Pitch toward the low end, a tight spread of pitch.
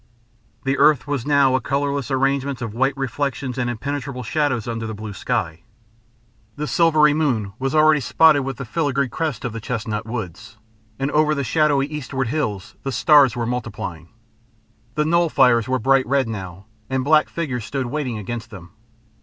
No: low, 130 Hz; average, 4.0 semitones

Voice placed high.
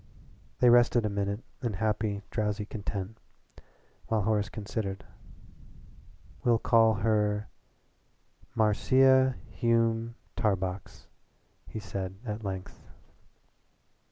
No: low, 110 Hz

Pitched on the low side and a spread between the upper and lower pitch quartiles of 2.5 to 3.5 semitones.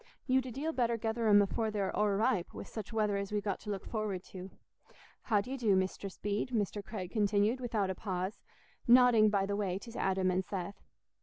No: high, 205 Hz; average, 2.8 semitones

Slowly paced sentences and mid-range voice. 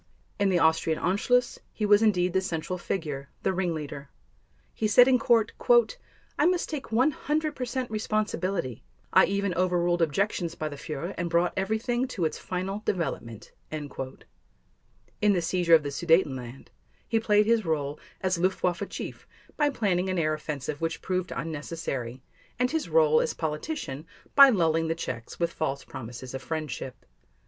No: average, 155 wpm; medium, 180 Hz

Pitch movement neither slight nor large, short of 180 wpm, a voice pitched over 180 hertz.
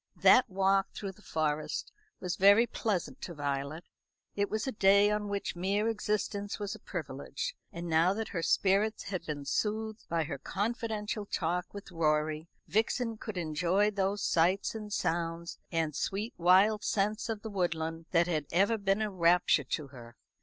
Yes: average, 4.1 semitones; average, 165 wpm; high, 190 Hz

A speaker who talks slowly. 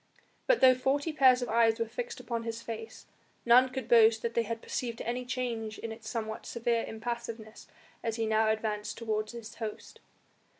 No: average, 180 wpm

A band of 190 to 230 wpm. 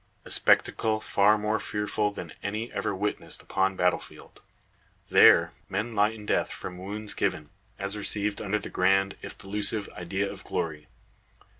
No: average, 155 wpm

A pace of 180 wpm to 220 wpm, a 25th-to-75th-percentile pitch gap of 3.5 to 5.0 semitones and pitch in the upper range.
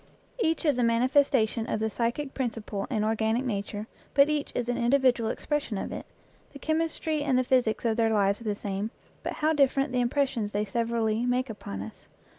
Yes: average, 195 wpm; average, 3.8 semitones; high, 240 Hz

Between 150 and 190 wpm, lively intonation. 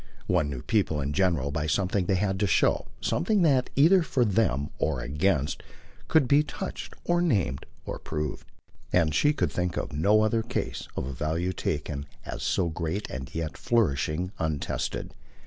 Yes: average, 170 wpm; wide, 6.9 semitones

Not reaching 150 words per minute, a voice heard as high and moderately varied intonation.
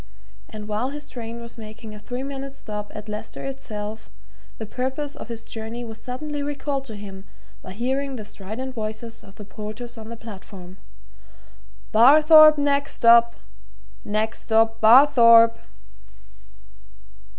Yes: average, 140 wpm; high, 230 Hz; average, 3.8 semitones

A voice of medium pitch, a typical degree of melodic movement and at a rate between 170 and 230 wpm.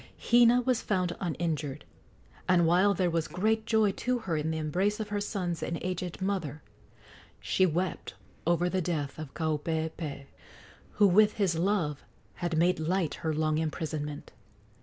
No: medium, 175 Hz; average, 3.8 semitones; average, 155 wpm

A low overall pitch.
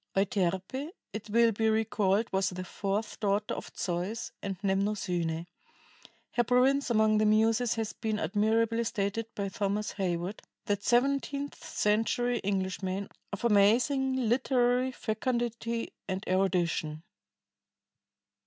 No: high, 215 Hz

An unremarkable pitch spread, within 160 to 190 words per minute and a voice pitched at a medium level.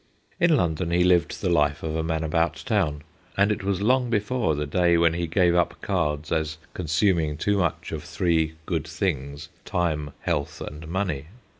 No: average, 3.3 semitones; average, 180 wpm; very low, 85 Hz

